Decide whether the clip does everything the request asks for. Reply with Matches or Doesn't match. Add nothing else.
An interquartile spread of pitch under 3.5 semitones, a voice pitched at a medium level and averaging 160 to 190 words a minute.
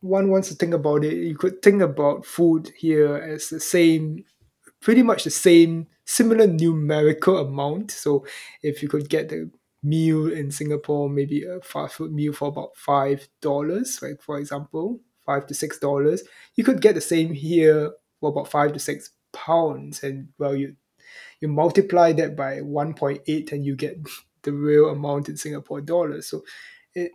Matches